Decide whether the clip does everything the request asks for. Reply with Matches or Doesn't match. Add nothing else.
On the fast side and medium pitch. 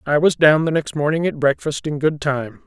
Matches